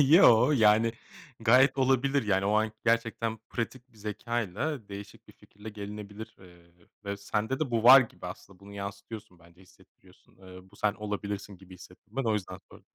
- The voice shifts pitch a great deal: No, average, 2.8 semitones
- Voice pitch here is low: Yes, low, 105 Hz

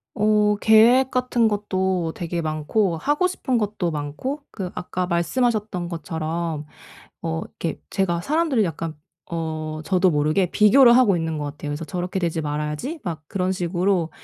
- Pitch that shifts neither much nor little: Yes, average, 4.8 semitones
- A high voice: No, medium, 180 Hz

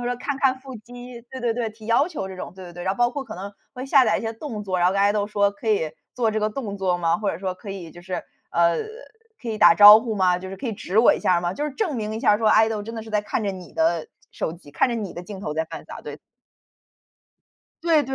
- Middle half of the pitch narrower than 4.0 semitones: No, average, 4.3 semitones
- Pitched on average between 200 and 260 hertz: Yes, high, 210 Hz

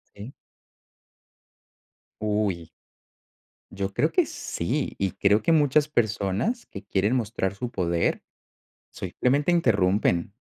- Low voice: Yes, low, 105 Hz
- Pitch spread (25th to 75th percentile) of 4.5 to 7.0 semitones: Yes, average, 5.0 semitones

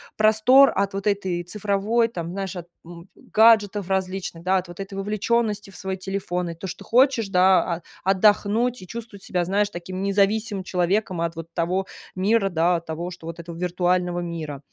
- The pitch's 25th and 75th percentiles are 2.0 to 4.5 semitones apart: Yes, average, 2.9 semitones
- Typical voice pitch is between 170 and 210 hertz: Yes, high, 190 Hz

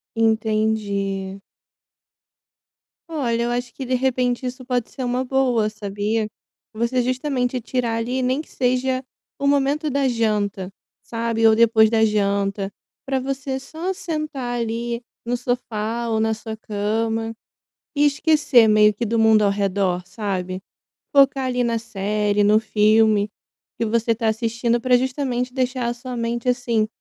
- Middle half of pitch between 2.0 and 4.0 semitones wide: Yes, average, 2.9 semitones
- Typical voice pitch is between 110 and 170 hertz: No, high, 235 Hz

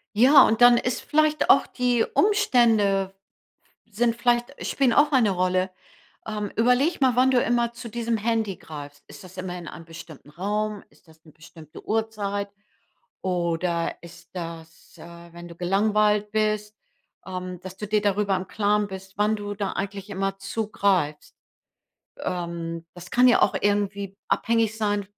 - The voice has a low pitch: No, high, 205 Hz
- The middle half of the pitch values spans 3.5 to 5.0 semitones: Yes, average, 3.9 semitones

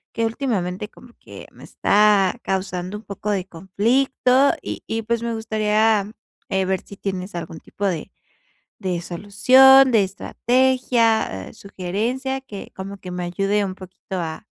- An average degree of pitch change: Yes, average, 3.6 semitones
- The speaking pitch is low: No, high, 205 Hz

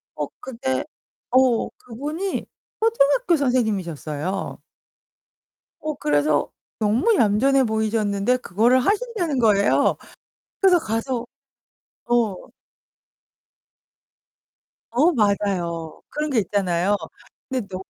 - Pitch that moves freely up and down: Yes, wide, 5.7 semitones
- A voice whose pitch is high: Yes, high, 230 Hz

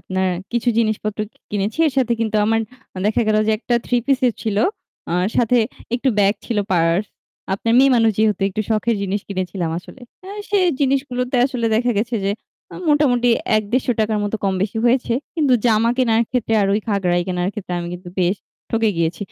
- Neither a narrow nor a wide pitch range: Yes, average, 3.7 semitones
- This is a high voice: Yes, high, 220 Hz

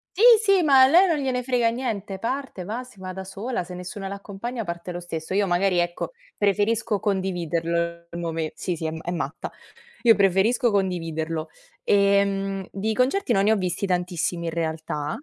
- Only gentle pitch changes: No, average, 4.7 semitones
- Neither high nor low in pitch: No, high, 195 Hz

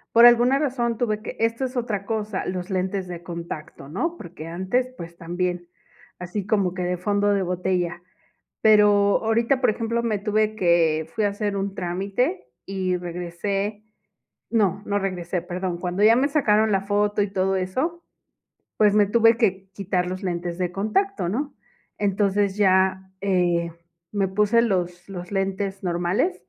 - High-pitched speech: Yes, high, 195 Hz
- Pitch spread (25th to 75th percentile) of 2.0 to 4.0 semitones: Yes, average, 3.1 semitones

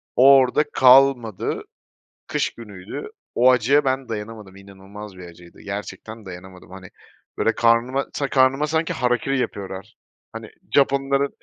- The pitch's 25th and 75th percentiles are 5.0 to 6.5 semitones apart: Yes, wide, 5.5 semitones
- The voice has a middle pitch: No, low, 115 Hz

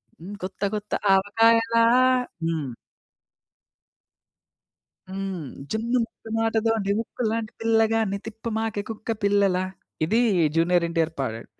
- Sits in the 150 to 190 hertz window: No, high, 215 Hz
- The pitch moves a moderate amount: Yes, average, 3.3 semitones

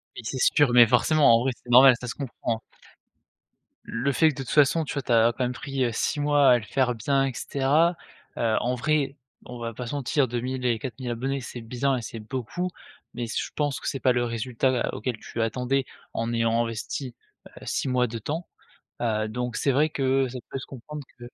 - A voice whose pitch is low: Yes, low, 125 Hz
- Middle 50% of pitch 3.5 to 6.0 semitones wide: No, narrow, 2.6 semitones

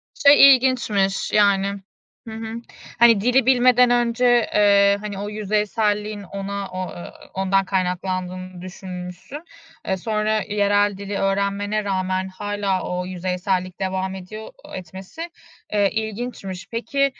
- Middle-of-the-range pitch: No, high, 200 Hz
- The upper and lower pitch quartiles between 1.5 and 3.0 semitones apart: Yes, narrow, 2.6 semitones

